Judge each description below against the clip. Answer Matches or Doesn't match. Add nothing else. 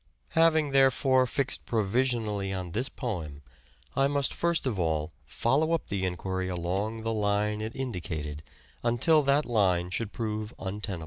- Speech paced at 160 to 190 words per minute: Doesn't match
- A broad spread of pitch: Matches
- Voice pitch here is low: Matches